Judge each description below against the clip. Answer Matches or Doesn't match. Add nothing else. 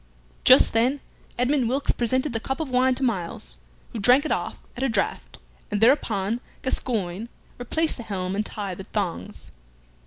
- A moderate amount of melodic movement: Matches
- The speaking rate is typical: Matches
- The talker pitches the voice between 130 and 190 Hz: Doesn't match